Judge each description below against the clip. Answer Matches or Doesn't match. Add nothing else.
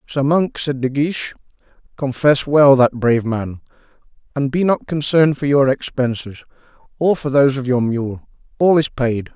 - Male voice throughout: Matches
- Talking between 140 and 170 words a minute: Matches